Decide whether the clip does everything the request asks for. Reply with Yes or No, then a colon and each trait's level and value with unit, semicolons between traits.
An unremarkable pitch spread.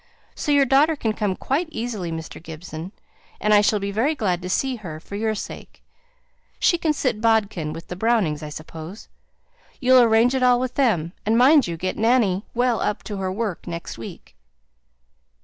No: wide, 5.7 semitones